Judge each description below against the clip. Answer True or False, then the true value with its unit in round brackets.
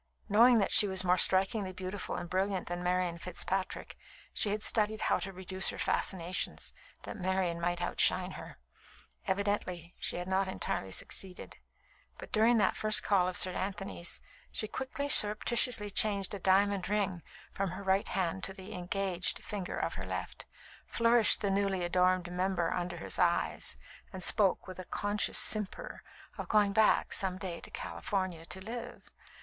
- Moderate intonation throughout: False (2.3 semitones)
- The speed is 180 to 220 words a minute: False (165 wpm)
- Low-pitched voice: False (190 Hz)